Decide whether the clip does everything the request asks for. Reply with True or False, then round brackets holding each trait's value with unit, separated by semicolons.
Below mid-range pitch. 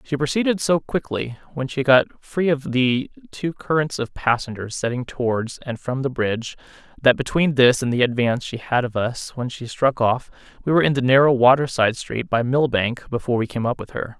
True (130 Hz)